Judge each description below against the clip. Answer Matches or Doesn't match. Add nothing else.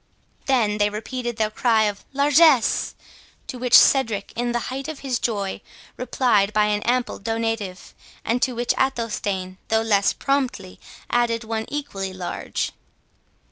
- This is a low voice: Doesn't match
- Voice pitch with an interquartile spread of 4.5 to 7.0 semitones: Doesn't match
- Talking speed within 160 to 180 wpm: Doesn't match